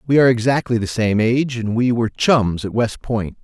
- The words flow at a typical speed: No, fast, 225 wpm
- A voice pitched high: No, low, 115 Hz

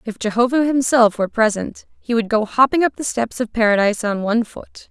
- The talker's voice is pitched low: No, high, 230 Hz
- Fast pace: Yes, fast, 210 wpm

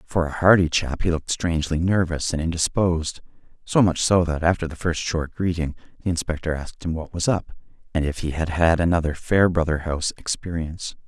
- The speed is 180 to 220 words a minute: Yes, average, 190 wpm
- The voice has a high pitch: No, very low, 85 Hz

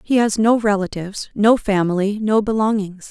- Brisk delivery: No, average, 155 wpm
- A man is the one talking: No, female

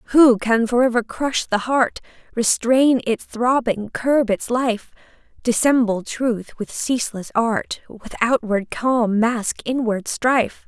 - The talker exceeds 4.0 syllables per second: No, 3.6 syllables/s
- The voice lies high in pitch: Yes, high, 235 Hz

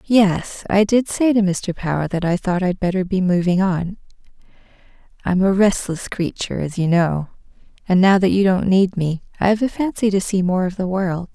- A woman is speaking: Yes, female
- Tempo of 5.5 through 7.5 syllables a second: No, 5.0 syllables/s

